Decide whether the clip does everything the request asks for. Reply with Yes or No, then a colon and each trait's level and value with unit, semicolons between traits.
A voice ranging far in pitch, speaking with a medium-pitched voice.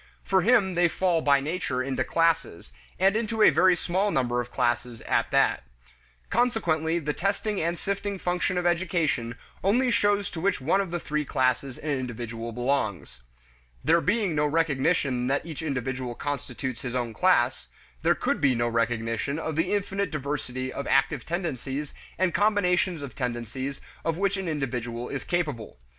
Yes: wide, 6.2 semitones; medium, 150 Hz